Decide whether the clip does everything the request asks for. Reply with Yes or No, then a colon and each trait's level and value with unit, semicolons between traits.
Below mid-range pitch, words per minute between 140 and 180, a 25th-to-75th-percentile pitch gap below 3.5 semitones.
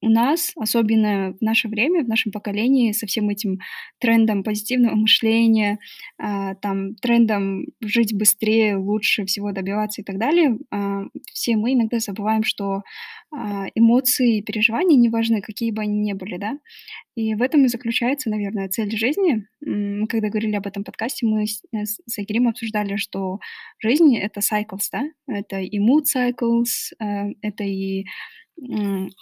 No: high, 220 Hz; average, 145 wpm; average, 2.7 semitones